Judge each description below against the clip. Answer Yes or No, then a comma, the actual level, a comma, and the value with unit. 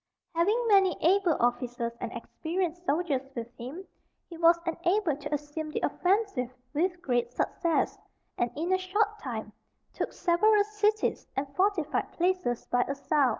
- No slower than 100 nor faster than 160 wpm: Yes, average, 145 wpm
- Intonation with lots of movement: Yes, wide, 5.7 semitones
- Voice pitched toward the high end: Yes, very high, 335 Hz